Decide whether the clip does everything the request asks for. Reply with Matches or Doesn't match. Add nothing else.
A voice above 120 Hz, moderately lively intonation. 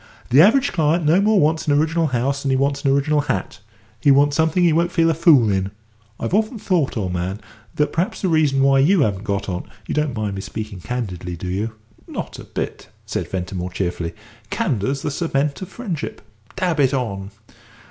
Doesn't match